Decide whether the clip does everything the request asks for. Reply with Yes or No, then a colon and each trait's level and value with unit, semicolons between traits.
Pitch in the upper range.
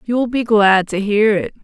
Yes: high, 210 Hz